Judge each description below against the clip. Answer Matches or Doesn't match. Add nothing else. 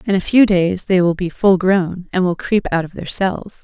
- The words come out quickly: Matches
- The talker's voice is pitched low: Doesn't match